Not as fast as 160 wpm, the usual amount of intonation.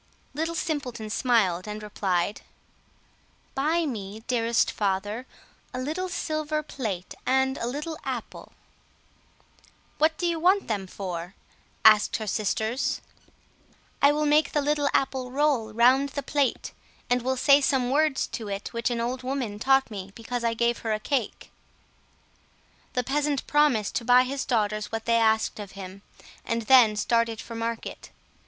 Yes: average, 150 wpm; average, 4.7 semitones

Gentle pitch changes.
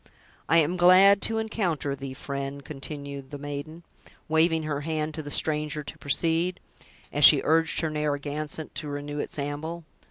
Yes: narrow, 2.2 semitones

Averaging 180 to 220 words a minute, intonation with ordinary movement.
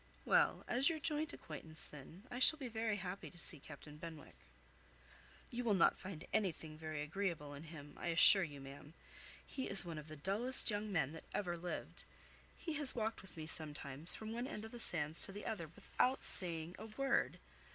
No: average, 195 wpm; wide, 5.9 semitones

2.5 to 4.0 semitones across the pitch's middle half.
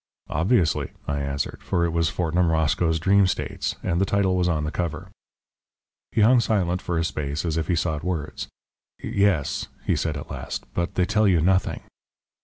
Yes: average, 2.9 semitones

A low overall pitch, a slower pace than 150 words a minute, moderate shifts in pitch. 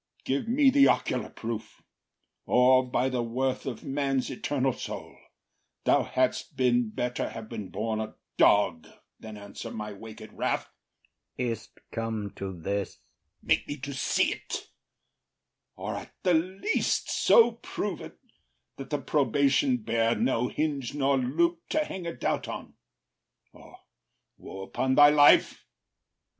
Yes: low, 130 Hz; average, 140 wpm; average, 4.6 semitones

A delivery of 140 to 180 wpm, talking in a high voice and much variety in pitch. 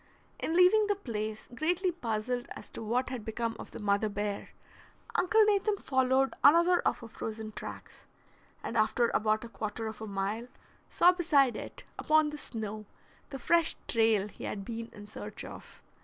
Yes: average, 170 wpm; high, 235 Hz; wide, 6.5 semitones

